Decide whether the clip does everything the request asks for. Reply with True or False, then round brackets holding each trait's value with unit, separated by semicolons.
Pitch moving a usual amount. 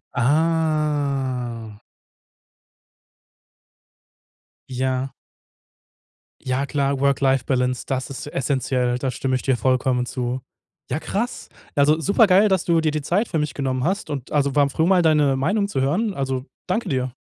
True (3.6 semitones)